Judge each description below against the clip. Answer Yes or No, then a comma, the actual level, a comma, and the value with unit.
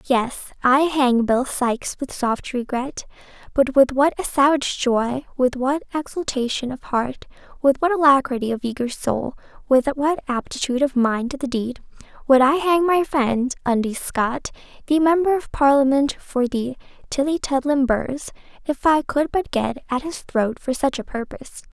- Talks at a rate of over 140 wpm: Yes, average, 165 wpm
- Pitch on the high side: Yes, very high, 270 Hz